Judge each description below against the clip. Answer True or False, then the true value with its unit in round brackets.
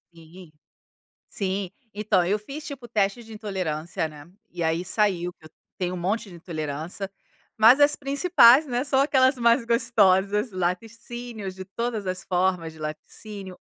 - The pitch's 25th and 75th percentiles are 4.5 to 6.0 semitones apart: True (4.8 semitones)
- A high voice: True (200 Hz)